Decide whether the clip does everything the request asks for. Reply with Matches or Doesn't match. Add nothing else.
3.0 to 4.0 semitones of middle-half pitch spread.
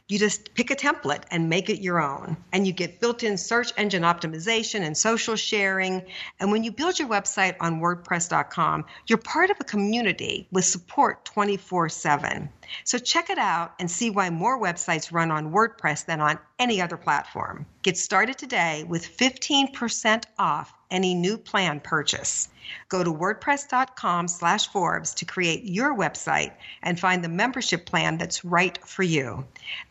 Doesn't match